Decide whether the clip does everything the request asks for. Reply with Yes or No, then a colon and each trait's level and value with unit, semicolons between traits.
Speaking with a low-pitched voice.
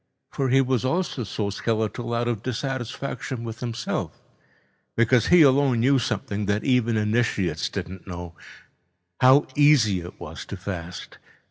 Yes: low, 115 Hz